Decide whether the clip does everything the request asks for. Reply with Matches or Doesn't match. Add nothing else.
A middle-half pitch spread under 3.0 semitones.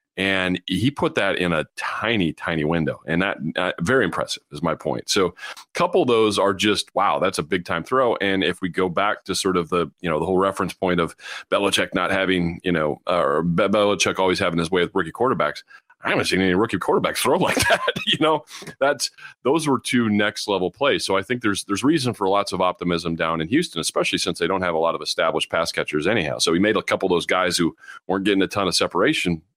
Matches